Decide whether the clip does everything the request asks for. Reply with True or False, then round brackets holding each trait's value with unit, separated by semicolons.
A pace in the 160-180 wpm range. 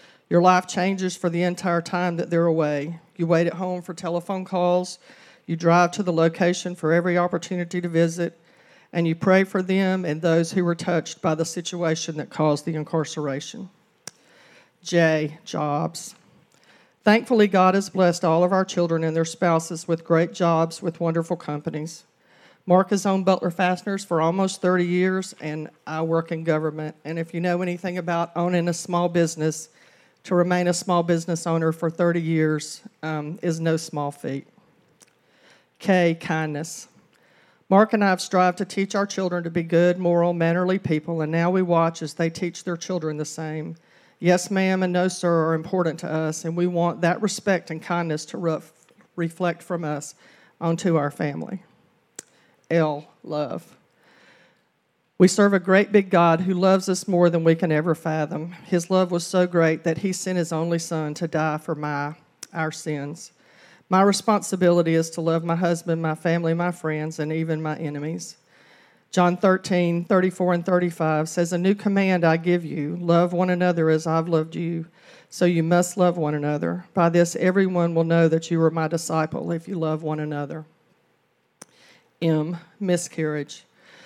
True (175 wpm)